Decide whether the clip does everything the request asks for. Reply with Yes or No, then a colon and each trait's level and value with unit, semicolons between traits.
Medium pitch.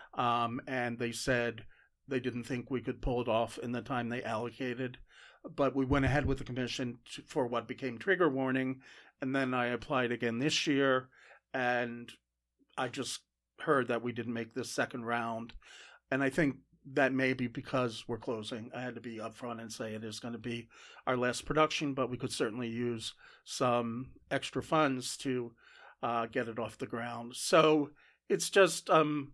No: low, 125 Hz